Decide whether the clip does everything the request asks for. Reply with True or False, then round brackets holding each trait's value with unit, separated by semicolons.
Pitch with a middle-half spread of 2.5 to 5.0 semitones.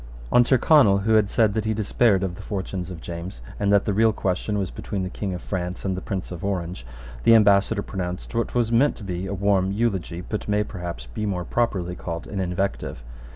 True (3.0 semitones)